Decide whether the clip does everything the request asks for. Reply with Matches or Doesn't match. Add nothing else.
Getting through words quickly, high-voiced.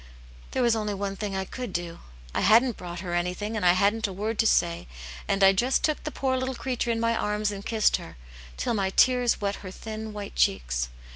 Matches